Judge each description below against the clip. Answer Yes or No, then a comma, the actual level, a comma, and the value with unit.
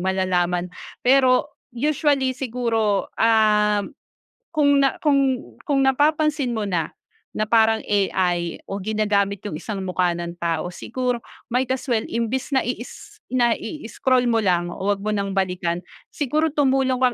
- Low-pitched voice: No, high, 225 Hz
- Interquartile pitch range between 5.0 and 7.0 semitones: Yes, average, 5.3 semitones